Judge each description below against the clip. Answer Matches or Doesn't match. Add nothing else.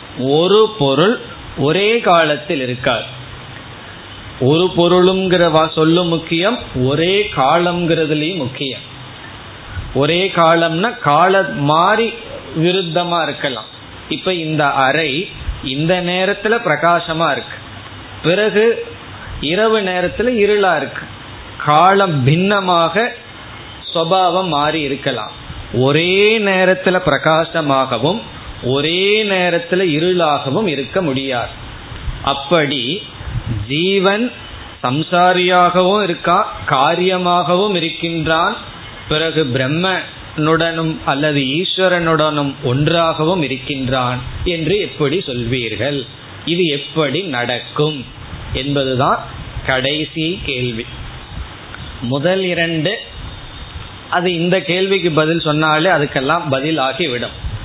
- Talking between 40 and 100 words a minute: Matches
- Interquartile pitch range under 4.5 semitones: Doesn't match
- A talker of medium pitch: Matches